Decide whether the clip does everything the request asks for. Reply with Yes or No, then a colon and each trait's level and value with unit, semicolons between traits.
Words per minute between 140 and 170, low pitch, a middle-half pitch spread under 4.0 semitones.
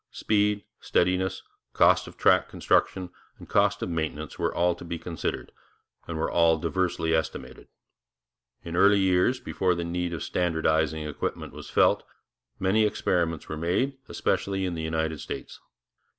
Yes: average, 150 wpm; very low, 85 Hz; average, 2.7 semitones